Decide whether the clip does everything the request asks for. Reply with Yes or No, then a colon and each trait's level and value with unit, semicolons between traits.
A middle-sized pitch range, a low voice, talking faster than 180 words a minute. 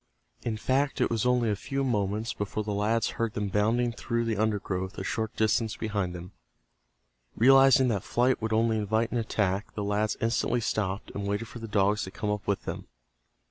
No: narrow, 2.2 semitones; low, 110 Hz; average, 195 wpm